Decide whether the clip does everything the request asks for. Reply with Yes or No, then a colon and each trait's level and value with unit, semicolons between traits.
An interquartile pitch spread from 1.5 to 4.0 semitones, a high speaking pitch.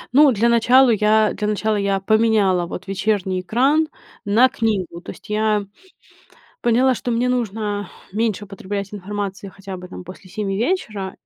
Yes: average, 2.9 semitones; high, 210 Hz